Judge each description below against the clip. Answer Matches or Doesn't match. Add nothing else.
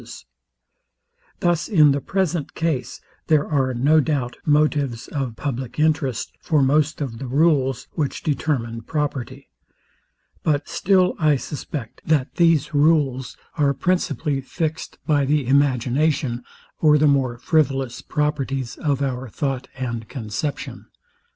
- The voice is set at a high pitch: Doesn't match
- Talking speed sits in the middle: Doesn't match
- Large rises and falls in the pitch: Doesn't match